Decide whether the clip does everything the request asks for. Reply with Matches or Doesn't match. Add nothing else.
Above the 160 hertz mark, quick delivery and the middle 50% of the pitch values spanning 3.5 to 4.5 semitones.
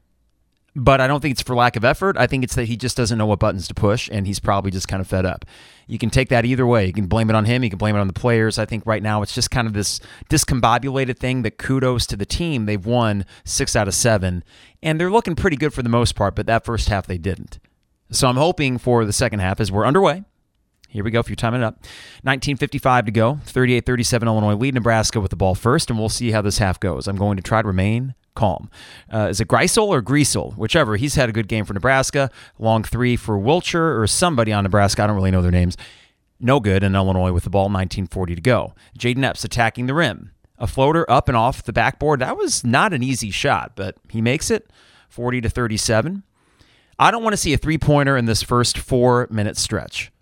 Doesn't match